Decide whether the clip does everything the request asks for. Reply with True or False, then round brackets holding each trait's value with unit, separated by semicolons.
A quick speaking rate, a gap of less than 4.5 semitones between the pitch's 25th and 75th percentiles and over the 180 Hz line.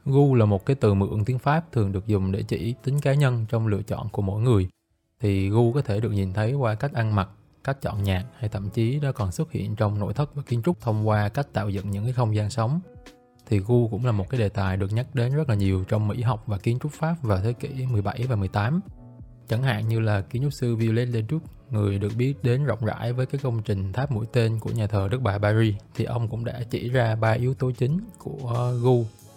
False (260 wpm; 3.5 semitones; 115 Hz)